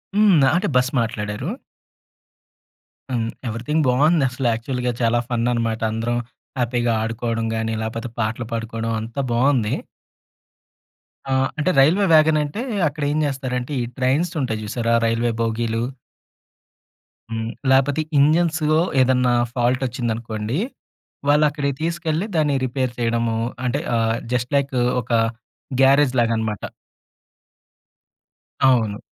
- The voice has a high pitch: No, low, 125 Hz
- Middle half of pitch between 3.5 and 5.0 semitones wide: Yes, average, 3.9 semitones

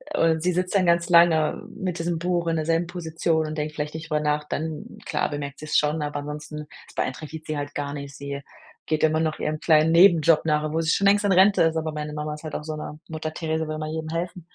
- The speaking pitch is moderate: Yes, medium, 155 Hz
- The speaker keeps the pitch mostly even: Yes, narrow, 1.7 semitones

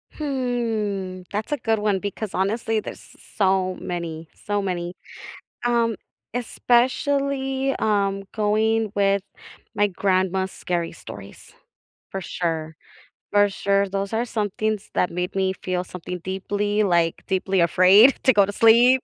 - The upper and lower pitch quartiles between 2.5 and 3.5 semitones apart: Yes, average, 3.2 semitones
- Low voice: No, high, 200 Hz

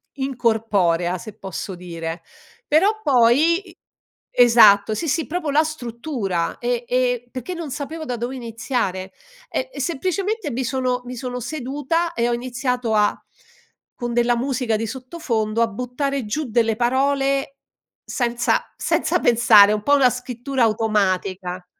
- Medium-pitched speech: No, high, 245 Hz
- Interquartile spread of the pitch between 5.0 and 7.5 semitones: No, average, 3.9 semitones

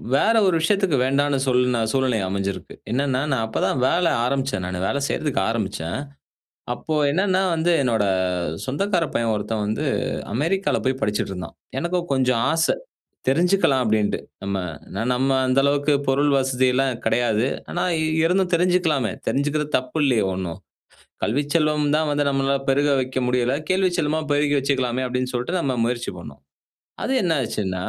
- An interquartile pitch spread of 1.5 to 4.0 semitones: No, average, 4.6 semitones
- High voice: No, low, 135 Hz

